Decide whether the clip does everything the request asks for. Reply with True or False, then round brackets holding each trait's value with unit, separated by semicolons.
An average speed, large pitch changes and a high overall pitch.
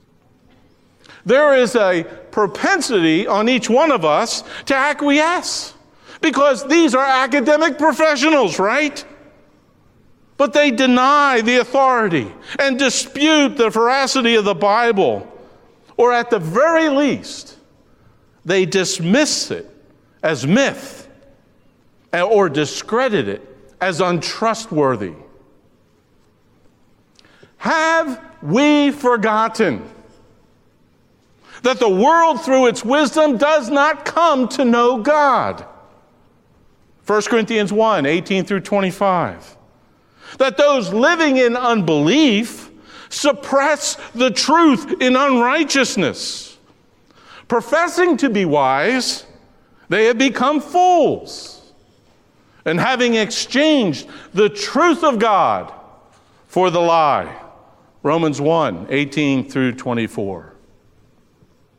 False (95 wpm; 6.4 semitones; 255 Hz)